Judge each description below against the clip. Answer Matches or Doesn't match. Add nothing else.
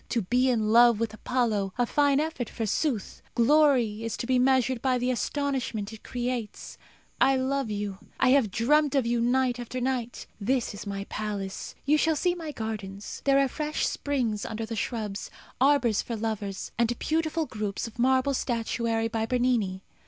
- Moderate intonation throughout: Matches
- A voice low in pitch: Doesn't match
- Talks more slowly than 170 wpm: Doesn't match